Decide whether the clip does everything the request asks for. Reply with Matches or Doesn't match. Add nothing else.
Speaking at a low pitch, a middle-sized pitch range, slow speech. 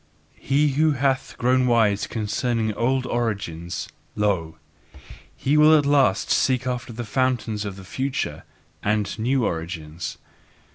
Matches